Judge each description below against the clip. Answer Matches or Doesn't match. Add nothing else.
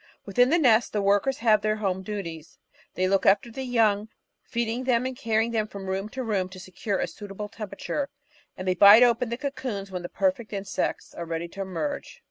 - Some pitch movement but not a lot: Matches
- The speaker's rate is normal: Doesn't match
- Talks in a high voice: Matches